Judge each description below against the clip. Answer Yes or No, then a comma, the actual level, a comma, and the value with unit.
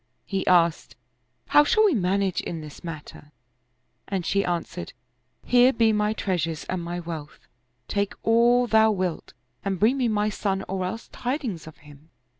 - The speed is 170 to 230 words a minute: Yes, average, 175 wpm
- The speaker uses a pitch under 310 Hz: Yes, high, 190 Hz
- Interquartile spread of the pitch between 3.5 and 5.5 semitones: Yes, average, 4.7 semitones